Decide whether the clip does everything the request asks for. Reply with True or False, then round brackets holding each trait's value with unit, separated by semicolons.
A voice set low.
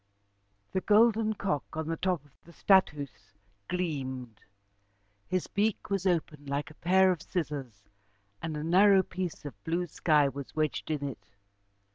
False (160 Hz)